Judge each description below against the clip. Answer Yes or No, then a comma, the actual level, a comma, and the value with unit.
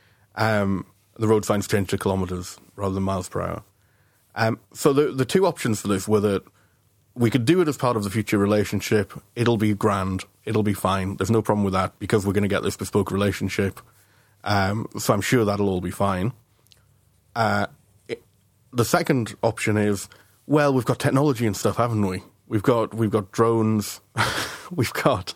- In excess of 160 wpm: Yes, average, 190 wpm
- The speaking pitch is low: Yes, low, 105 Hz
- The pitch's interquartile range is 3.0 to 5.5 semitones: No, narrow, 2.4 semitones